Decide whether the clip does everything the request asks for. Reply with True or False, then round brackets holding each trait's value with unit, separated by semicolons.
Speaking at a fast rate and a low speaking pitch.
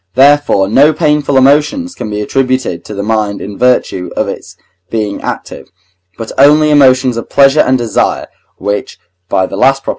False (170 wpm; 130 Hz)